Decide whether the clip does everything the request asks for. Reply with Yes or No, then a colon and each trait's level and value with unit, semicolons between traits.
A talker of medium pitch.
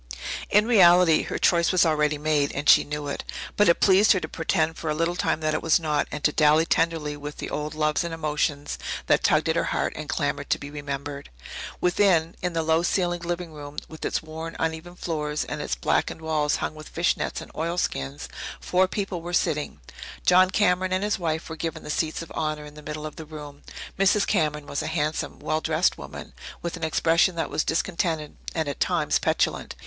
Yes: medium, 160 Hz